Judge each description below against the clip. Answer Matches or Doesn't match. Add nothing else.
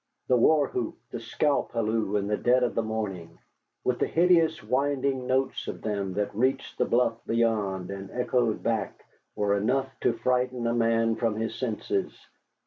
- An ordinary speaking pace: Matches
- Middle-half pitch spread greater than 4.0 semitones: Doesn't match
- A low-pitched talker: Matches